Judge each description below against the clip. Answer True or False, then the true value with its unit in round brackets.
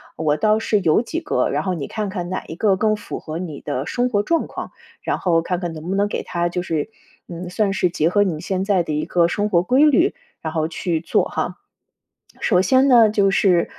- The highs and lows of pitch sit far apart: False (3.9 semitones)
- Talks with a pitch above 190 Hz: False (185 Hz)